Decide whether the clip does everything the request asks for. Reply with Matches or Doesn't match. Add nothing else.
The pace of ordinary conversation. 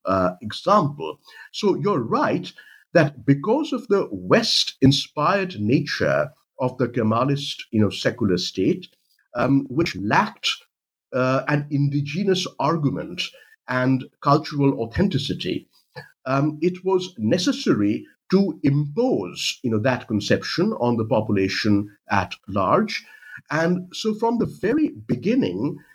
Doesn't match